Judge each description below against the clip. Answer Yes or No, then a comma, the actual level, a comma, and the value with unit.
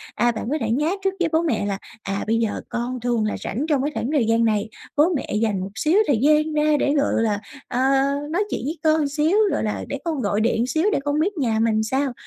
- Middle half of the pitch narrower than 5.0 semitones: No, average, 5.3 semitones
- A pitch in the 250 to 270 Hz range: Yes, very high, 260 Hz